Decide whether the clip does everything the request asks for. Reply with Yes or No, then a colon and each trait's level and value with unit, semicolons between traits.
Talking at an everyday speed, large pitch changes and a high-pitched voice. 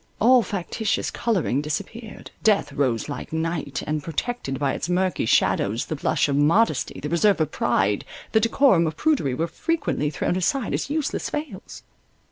No: average, 155 wpm; wide, 7.7 semitones; medium, 165 Hz